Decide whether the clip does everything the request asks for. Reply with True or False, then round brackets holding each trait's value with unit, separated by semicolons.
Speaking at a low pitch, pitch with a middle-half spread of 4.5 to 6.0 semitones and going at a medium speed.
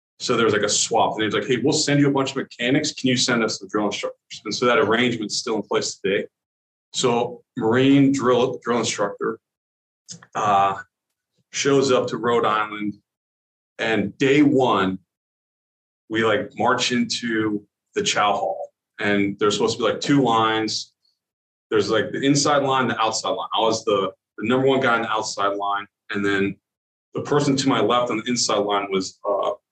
True (120 Hz; 5.0 semitones; 190 wpm)